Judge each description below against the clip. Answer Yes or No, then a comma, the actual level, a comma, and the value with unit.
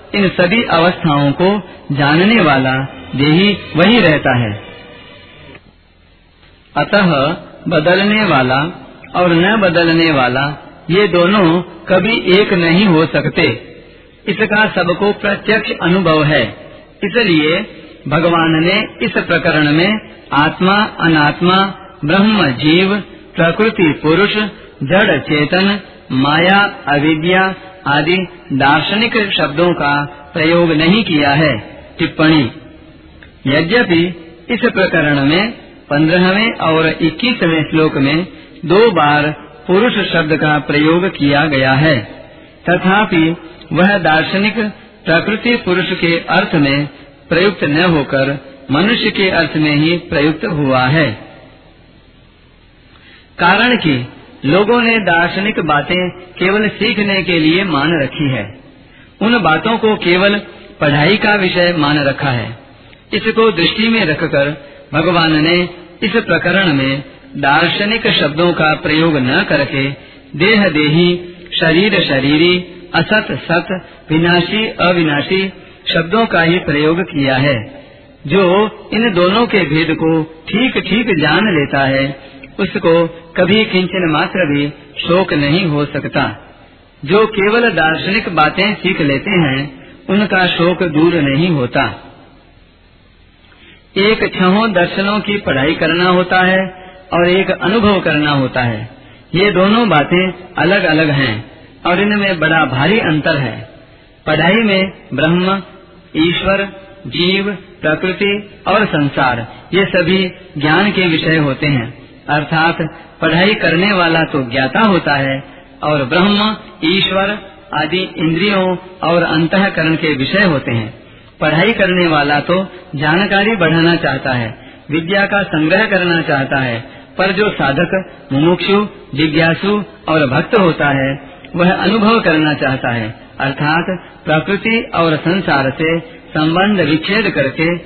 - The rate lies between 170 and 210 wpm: No, average, 120 wpm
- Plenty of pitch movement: No, average, 4.5 semitones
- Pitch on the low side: No, medium, 170 Hz